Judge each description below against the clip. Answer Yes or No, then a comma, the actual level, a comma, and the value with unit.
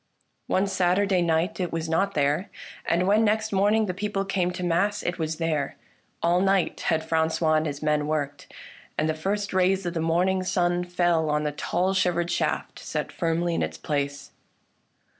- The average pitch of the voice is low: No, medium, 175 Hz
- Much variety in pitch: No, average, 3.1 semitones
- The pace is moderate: Yes, average, 180 wpm